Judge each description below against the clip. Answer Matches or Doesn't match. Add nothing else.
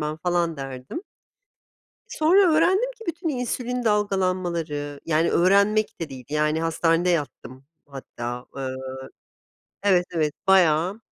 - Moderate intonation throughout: Doesn't match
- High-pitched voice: Doesn't match